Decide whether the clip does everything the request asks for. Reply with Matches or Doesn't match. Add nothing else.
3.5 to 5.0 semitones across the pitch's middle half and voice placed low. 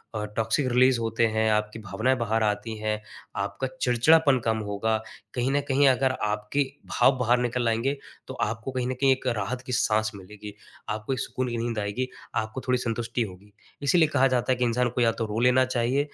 Doesn't match